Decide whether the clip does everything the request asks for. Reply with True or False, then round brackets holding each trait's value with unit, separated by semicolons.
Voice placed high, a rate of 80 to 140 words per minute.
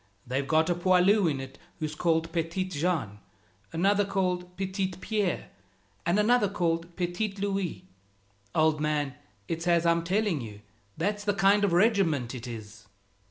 False (175 Hz; 135 wpm)